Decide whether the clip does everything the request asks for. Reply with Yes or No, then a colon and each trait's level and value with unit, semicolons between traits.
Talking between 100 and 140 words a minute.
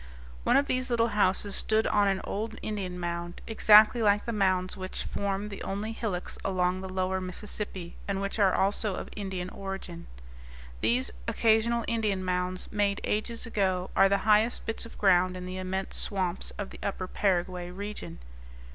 No: average, 170 wpm